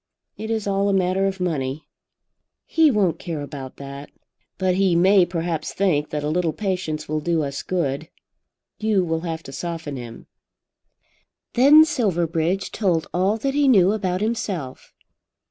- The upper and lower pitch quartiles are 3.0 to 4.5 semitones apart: Yes, average, 4.2 semitones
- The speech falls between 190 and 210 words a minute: No, average, 155 wpm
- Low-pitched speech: No, medium, 175 Hz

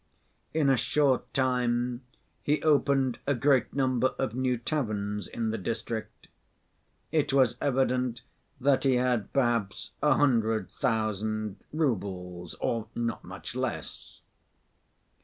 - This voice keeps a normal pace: No, slow, 120 wpm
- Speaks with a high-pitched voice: No, low, 125 Hz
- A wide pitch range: No, average, 3.4 semitones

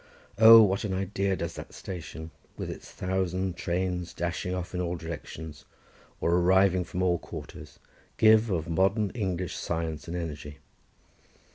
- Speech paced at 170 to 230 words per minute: No, average, 145 wpm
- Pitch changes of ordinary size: No, narrow, 2.1 semitones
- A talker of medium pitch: No, very low, 90 Hz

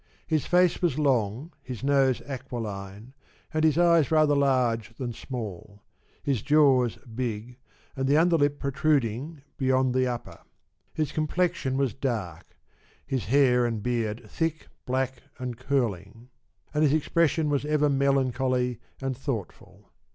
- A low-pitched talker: Yes, low, 130 Hz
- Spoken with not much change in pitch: No, average, 3.5 semitones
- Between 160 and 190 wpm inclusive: No, slow, 135 wpm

